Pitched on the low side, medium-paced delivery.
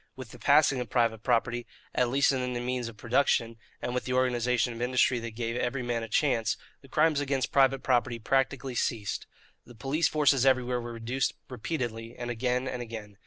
Yes: low, 125 Hz; average, 195 wpm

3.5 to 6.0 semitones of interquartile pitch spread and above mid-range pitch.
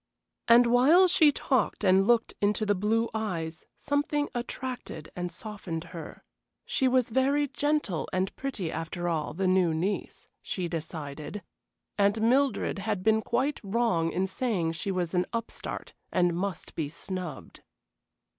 Yes: wide, 5.6 semitones; high, 200 Hz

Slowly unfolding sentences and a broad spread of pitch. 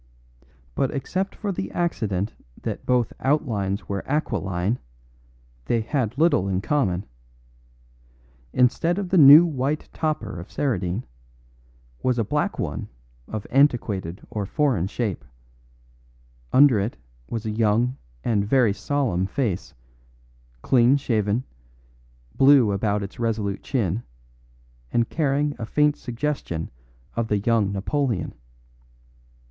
Yes: slow, 115 wpm; wide, 5.8 semitones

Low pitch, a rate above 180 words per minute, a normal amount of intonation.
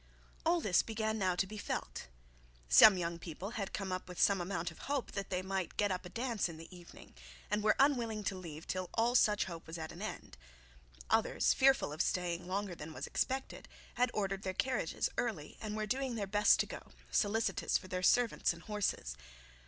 No: high, 195 Hz; average, 200 wpm; average, 3.7 semitones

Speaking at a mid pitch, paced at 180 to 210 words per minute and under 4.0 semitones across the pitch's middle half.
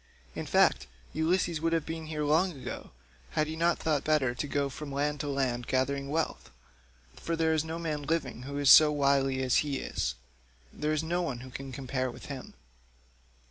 Yes: medium, 145 Hz; average, 190 wpm; average, 2.8 semitones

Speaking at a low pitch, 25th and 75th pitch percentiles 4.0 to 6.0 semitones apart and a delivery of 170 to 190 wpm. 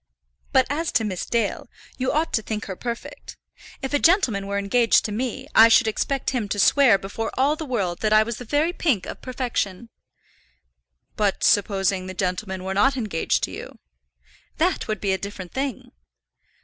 No: high, 220 Hz; average, 4.7 semitones; average, 185 wpm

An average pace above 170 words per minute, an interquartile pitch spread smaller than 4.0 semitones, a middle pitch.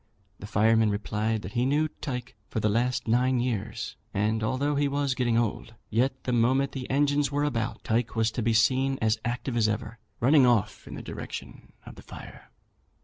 No: average, 195 wpm; average, 3.0 semitones; low, 120 Hz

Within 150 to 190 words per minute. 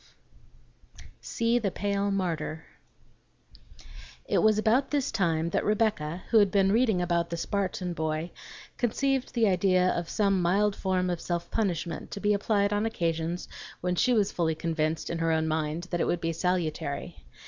Yes: average, 170 wpm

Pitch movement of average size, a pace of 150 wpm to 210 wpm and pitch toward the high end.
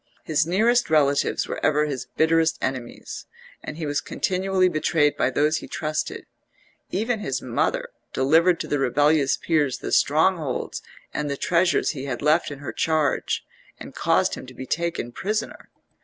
No: average, 3.4 semitones; average, 160 wpm; medium, 155 Hz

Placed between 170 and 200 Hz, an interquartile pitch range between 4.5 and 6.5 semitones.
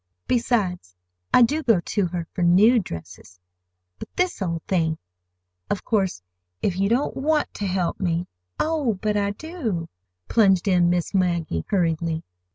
Yes: high, 190 Hz; average, 4.9 semitones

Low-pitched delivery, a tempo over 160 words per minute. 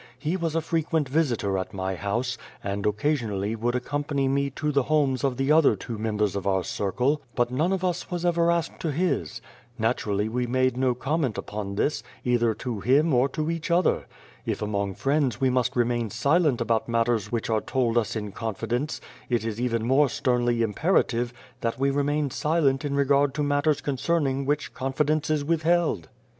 Yes: low, 130 Hz; average, 190 wpm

